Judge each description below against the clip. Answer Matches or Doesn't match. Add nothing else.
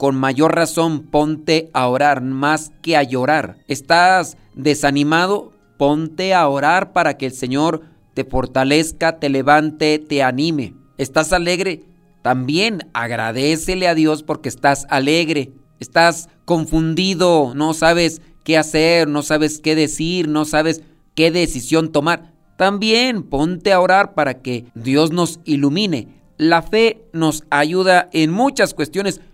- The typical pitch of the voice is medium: Matches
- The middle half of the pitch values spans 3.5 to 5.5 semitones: Doesn't match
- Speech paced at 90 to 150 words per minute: Matches